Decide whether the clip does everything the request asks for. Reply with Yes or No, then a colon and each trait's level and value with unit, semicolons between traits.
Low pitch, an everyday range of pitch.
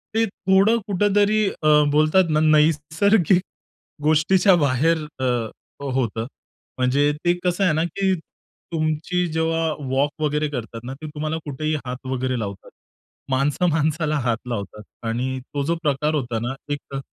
No: medium, 150 Hz; average, 4.1 semitones